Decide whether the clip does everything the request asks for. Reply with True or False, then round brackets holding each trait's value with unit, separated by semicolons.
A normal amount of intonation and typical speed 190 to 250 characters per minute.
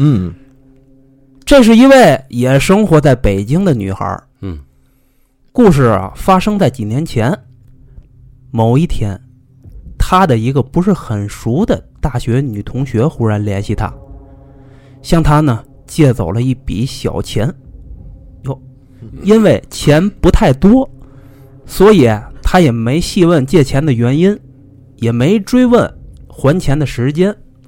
False (4.8 semitones; 180 characters per minute)